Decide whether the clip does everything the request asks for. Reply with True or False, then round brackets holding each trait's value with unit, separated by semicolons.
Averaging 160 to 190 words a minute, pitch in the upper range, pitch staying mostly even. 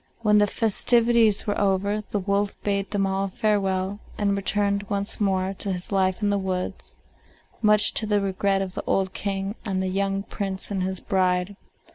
True (180 wpm; 200 Hz; 1.3 semitones)